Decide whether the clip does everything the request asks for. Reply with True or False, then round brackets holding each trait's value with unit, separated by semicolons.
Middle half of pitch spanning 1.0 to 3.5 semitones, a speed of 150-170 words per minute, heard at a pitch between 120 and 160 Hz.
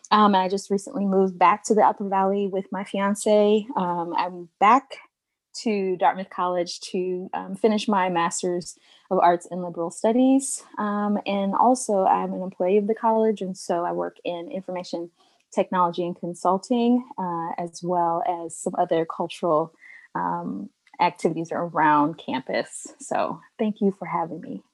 False (3.0 semitones; 155 wpm; 185 Hz)